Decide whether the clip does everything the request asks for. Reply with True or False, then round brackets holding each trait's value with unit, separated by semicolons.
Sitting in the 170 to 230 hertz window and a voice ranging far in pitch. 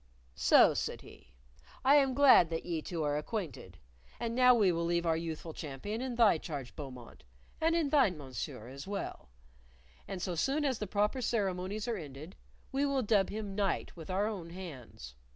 True (190 Hz; 6.5 semitones)